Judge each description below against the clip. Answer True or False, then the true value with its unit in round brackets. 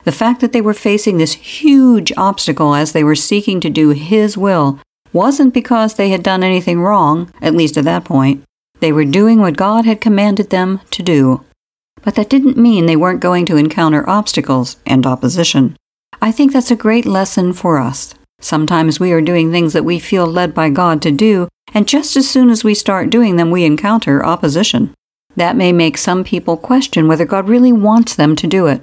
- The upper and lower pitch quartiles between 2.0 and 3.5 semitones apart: False (5.3 semitones)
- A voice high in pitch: False (180 Hz)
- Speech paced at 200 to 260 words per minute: True (205 wpm)